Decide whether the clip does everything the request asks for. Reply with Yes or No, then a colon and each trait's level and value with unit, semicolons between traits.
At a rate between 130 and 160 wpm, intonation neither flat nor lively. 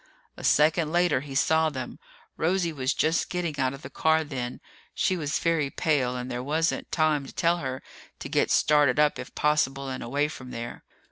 No: average, 195 wpm; average, 3.3 semitones